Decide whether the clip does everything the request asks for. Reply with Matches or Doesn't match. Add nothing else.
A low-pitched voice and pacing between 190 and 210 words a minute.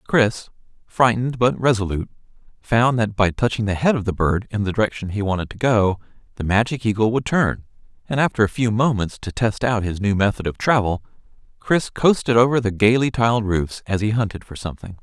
Matches